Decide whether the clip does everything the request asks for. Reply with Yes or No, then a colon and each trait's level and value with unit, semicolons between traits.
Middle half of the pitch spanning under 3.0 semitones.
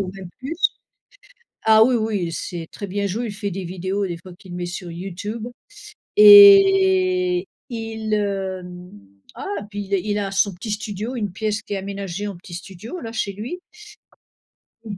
No: average, 3.3 semitones